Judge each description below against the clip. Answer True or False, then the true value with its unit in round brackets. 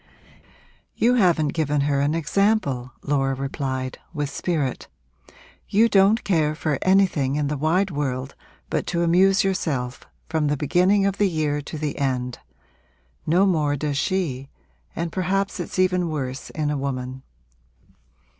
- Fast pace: False (145 wpm)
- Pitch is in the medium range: True (155 Hz)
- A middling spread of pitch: True (5.0 semitones)